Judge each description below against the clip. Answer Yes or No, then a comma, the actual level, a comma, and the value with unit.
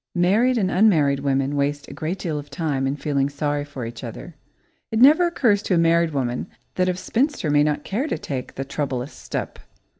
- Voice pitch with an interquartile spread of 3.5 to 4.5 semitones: No, average, 5.2 semitones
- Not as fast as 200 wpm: No, fast, 205 wpm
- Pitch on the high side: No, medium, 150 Hz